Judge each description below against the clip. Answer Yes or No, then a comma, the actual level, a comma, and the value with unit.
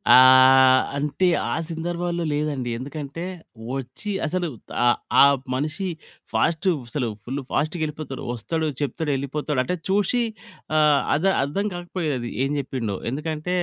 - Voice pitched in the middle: Yes, medium, 150 Hz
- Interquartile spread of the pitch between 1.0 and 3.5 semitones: No, average, 4.3 semitones